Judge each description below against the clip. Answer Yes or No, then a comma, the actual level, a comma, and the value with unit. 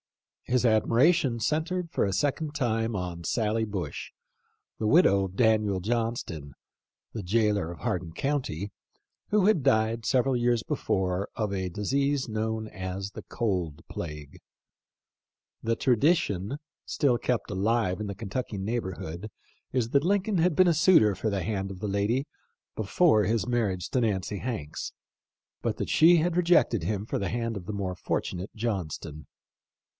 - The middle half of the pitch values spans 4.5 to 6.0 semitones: Yes, average, 4.8 semitones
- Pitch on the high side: No, low, 110 Hz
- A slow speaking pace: No, average, 160 wpm